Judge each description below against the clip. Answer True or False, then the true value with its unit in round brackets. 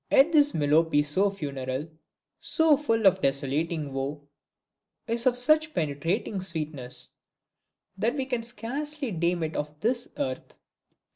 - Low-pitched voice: False (180 Hz)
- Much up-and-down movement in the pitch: True (9.0 semitones)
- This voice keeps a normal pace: False (130 wpm)